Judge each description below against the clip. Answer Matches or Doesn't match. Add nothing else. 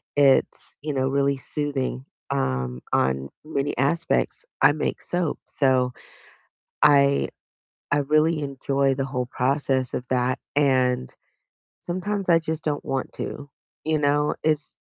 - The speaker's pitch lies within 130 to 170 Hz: Matches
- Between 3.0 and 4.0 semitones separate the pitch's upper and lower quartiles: Doesn't match